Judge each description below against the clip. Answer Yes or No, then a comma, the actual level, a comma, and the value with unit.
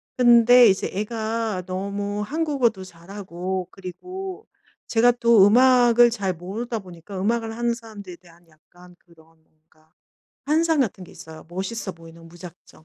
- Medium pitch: No, high, 200 Hz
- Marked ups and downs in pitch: No, average, 5.0 semitones